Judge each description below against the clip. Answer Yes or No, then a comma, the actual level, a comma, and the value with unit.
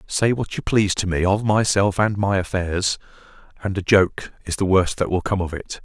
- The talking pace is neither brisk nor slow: No, fast, 225 wpm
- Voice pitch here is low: Yes, very low, 95 Hz